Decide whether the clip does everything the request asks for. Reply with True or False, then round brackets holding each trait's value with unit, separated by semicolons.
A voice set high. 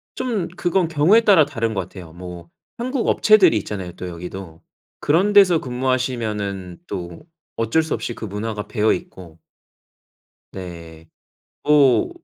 False (110 Hz)